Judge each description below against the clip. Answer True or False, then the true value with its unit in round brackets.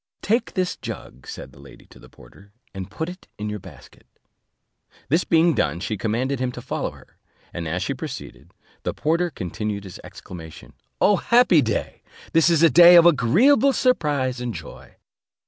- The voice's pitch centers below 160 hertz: True (135 Hz)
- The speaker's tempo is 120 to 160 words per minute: False (175 wpm)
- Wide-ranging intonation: True (9.0 semitones)